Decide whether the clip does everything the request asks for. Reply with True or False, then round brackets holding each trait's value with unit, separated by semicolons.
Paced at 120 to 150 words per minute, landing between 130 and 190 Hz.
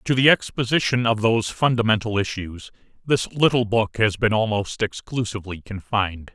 False (140 wpm; 110 Hz)